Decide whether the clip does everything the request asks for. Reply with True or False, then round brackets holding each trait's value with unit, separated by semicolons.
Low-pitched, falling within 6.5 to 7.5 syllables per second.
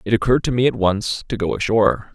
True (110 Hz; 6.7 syllables/s)